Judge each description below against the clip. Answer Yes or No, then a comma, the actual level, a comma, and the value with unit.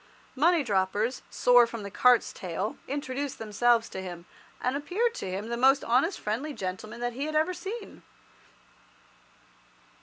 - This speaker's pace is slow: No, average, 150 wpm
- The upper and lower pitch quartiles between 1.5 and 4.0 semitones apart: No, wide, 5.4 semitones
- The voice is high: Yes, high, 245 Hz